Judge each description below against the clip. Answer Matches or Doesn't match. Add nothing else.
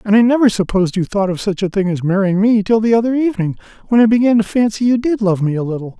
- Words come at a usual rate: Doesn't match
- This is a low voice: Doesn't match